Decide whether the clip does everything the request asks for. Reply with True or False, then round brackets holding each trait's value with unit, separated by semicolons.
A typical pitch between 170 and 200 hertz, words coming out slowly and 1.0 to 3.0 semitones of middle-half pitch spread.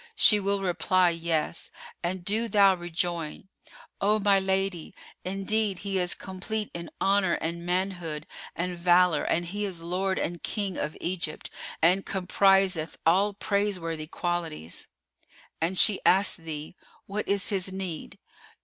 True (185 Hz; 130 wpm; 2.5 semitones)